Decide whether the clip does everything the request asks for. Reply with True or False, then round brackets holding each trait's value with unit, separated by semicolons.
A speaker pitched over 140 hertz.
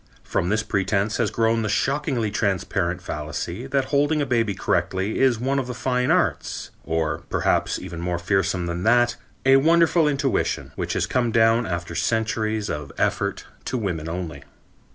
False (110 Hz)